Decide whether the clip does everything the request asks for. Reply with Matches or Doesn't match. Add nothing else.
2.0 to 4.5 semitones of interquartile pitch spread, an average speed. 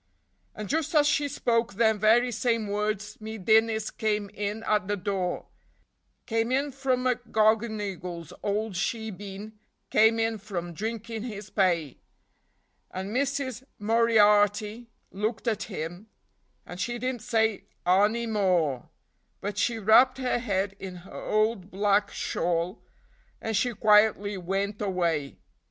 Doesn't match